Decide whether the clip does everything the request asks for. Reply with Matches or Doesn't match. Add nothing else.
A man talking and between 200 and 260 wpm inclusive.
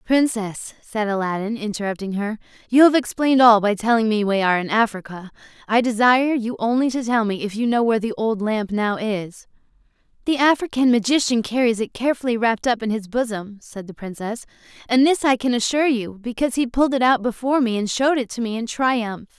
Doesn't match